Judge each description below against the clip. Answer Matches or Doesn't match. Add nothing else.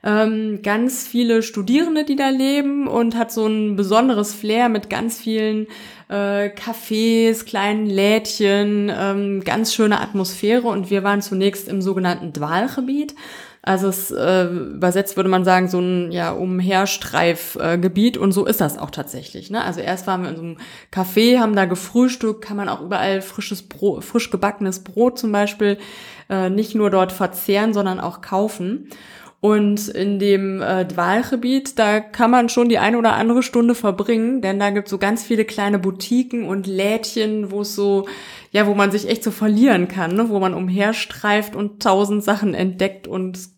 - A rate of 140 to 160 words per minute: Doesn't match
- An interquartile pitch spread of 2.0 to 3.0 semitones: Matches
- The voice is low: Doesn't match